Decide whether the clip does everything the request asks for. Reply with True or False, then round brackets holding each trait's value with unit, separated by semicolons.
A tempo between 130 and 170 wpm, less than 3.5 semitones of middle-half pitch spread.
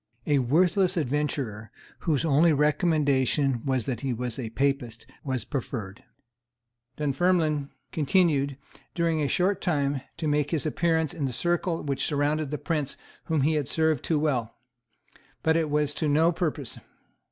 True (150 wpm; 3.1 semitones)